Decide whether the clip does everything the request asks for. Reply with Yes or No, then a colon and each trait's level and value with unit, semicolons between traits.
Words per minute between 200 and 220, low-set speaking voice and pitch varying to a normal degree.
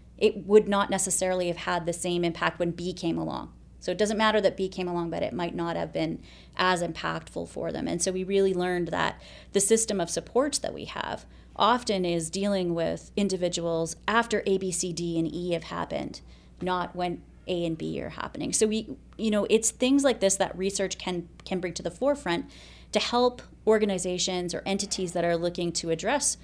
No: fast, 205 wpm; medium, 185 Hz; average, 3.3 semitones